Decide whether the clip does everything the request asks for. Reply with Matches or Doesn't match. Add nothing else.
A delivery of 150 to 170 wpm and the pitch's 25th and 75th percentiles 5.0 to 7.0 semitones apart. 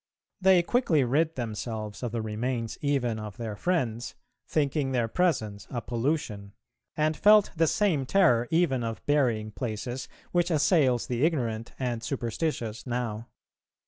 Doesn't match